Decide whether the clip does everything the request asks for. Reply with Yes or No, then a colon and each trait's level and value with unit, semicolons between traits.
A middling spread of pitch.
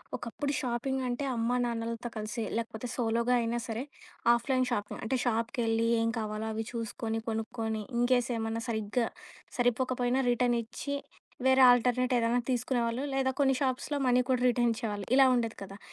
No: narrow, 1.9 semitones